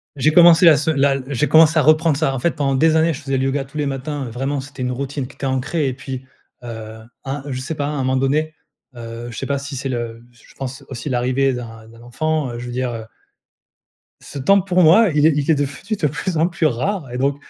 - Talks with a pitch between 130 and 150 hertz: Yes, medium, 140 Hz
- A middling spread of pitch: Yes, average, 3.5 semitones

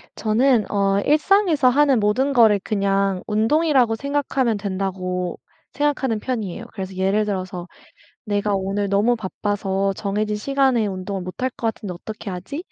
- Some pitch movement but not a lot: Yes, average, 4.6 semitones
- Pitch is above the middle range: Yes, high, 210 Hz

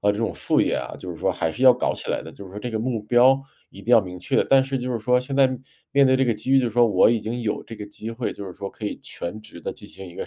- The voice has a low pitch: Yes, low, 115 Hz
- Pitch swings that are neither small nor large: Yes, average, 3.5 semitones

